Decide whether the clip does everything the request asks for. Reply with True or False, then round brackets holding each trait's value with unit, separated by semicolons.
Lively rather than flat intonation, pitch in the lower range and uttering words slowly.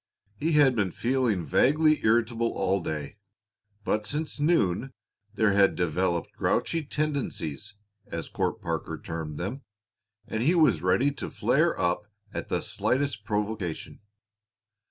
True (7.4 semitones; 110 Hz; 130 wpm)